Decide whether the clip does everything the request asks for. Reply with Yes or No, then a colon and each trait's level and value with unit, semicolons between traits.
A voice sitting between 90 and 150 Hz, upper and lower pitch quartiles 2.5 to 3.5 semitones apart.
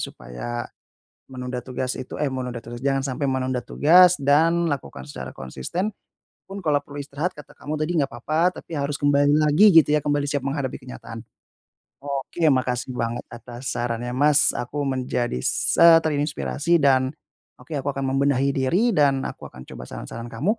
Yes: medium, 140 Hz; average, 3.1 semitones